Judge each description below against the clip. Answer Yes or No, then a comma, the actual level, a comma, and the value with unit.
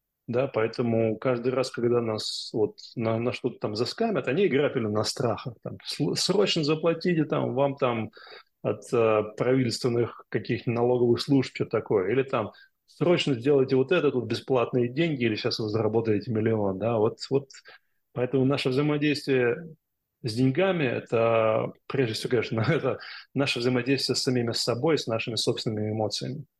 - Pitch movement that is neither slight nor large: Yes, average, 3.4 semitones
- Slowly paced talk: No, average, 150 wpm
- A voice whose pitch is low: Yes, low, 125 Hz